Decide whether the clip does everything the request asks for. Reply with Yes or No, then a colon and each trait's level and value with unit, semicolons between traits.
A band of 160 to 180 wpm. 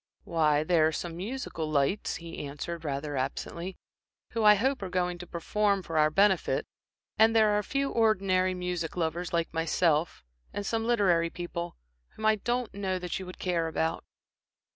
Yes: average, 175 wpm